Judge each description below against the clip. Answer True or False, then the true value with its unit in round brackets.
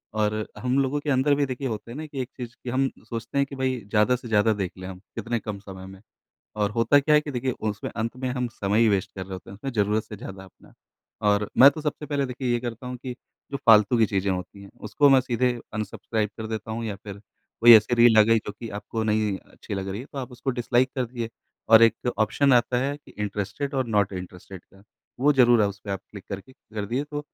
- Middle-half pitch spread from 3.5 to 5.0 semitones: True (3.9 semitones)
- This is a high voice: False (115 Hz)